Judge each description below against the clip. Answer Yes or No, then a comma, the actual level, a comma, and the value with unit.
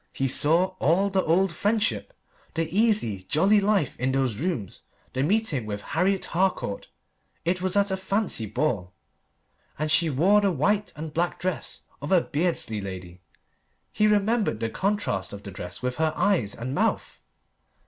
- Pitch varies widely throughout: Yes, wide, 8.1 semitones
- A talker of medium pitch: Yes, medium, 165 Hz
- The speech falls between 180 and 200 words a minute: No, average, 160 wpm